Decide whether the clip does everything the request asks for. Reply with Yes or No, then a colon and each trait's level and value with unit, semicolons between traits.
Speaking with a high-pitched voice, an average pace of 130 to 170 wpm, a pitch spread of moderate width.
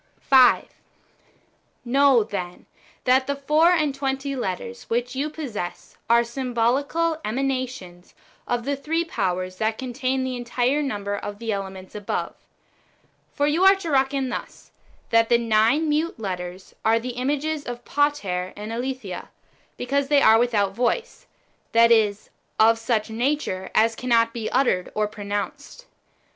Yes: high, 240 Hz; average, 150 wpm; average, 4.5 semitones